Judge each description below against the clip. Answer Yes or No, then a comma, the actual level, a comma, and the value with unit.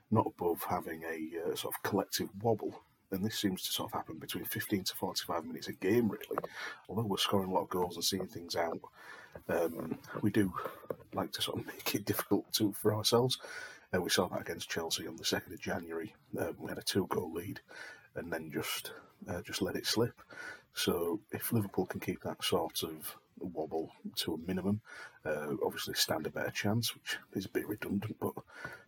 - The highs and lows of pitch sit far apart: No, average, 4.2 semitones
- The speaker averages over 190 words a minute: Yes, average, 200 wpm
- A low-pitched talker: Yes, low, 105 Hz